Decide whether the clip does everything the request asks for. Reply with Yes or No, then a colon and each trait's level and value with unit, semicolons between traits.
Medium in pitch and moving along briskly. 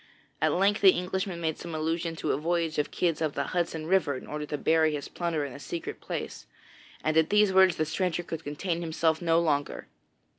Yes: medium, 165 Hz; fast, 215 wpm